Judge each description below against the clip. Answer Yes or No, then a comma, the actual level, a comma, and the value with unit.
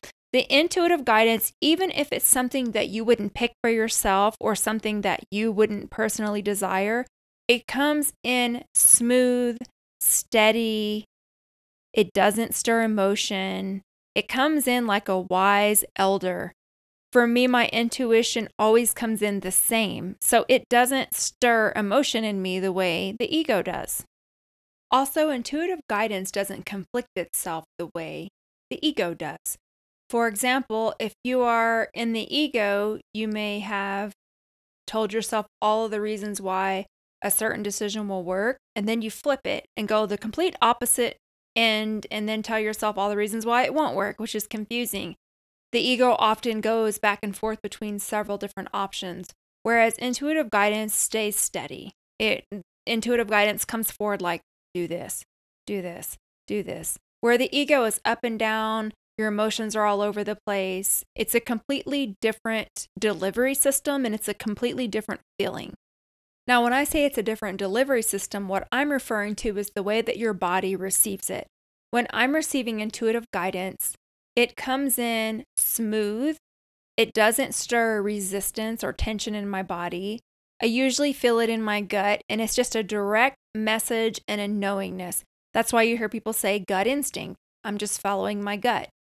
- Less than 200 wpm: Yes, average, 160 wpm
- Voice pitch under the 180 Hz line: No, high, 220 Hz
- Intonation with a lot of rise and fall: No, average, 2.8 semitones